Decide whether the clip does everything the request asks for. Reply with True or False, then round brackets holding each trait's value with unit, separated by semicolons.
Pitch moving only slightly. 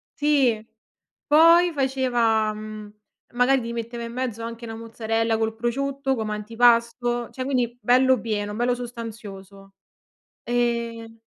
True (2.1 semitones)